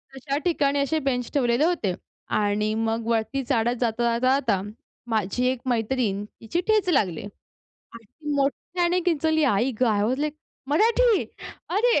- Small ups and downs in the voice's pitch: No, wide, 5.4 semitones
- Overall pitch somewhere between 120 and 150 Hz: No, very high, 255 Hz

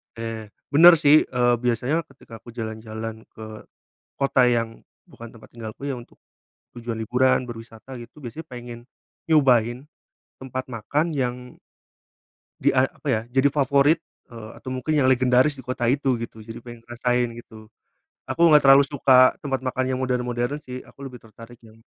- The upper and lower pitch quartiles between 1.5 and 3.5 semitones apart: Yes, narrow, 2.5 semitones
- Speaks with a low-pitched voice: Yes, low, 125 Hz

